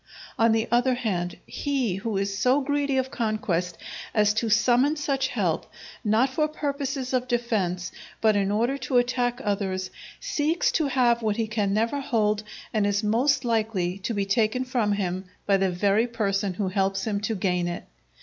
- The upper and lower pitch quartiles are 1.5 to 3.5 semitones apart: No, average, 4.2 semitones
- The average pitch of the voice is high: Yes, high, 220 Hz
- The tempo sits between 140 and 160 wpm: No, average, 180 wpm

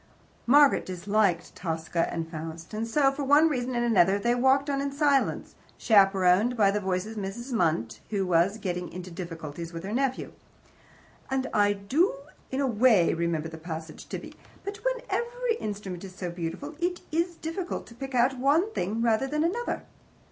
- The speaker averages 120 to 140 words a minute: No, average, 175 wpm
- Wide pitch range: Yes, wide, 7.4 semitones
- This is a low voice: No, high, 215 Hz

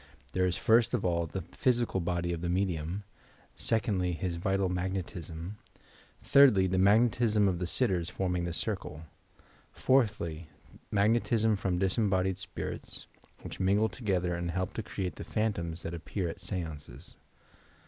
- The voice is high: No, very low, 95 Hz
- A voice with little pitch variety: No, average, 3.3 semitones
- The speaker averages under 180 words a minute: Yes, average, 145 wpm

